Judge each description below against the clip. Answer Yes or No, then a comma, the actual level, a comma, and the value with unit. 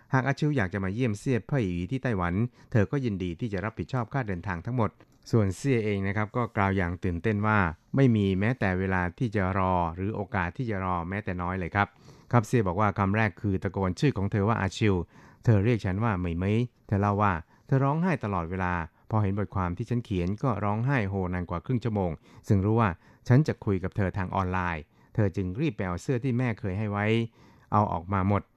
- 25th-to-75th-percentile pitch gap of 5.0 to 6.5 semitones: No, average, 4.3 semitones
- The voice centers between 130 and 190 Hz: No, low, 105 Hz